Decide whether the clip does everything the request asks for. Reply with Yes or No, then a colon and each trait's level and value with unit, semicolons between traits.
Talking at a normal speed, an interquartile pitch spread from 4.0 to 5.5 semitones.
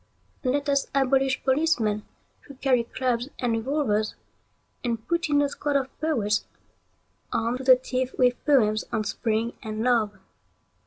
No: average, 145 wpm; average, 3.6 semitones